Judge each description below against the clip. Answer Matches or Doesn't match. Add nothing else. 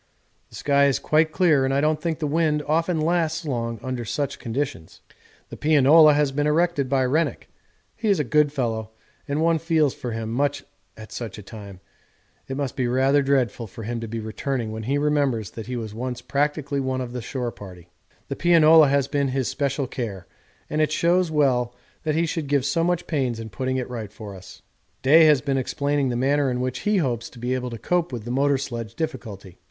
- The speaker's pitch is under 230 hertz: Matches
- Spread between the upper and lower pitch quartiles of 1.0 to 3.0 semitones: Doesn't match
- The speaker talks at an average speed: Doesn't match